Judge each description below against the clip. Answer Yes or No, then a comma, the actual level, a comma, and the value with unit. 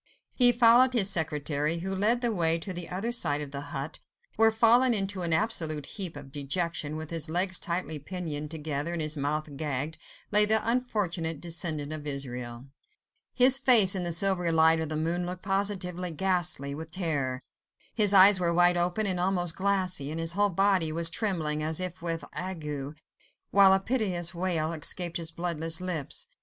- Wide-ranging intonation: No, average, 3.8 semitones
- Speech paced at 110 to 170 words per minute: No, average, 180 wpm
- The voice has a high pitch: No, medium, 170 Hz